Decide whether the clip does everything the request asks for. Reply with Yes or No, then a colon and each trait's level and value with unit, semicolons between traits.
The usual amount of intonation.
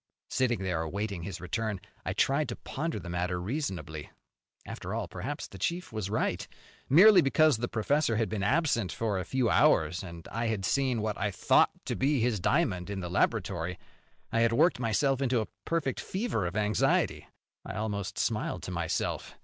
No: wide, 6.0 semitones